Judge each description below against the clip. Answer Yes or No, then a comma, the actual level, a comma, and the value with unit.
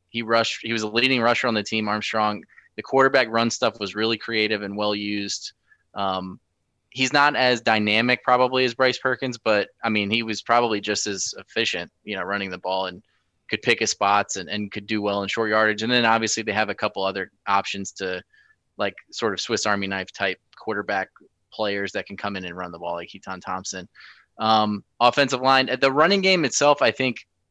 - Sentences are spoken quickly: Yes, fast, 210 wpm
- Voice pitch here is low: Yes, low, 110 Hz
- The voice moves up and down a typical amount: Yes, average, 3.0 semitones